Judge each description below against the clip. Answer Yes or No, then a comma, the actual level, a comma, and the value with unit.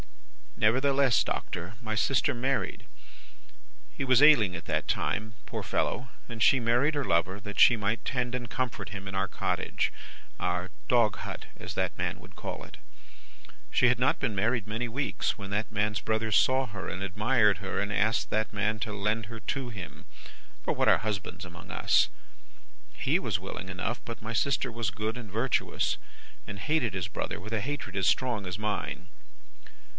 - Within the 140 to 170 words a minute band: No, average, 180 wpm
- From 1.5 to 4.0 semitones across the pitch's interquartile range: Yes, average, 3.6 semitones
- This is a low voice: Yes, low, 110 Hz